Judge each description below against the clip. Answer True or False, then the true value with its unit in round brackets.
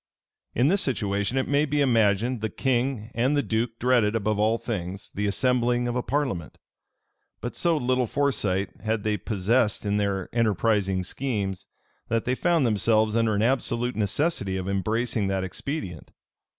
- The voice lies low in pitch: True (115 Hz)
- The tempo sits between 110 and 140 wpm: False (160 wpm)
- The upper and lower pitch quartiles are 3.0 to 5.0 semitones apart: True (3.8 semitones)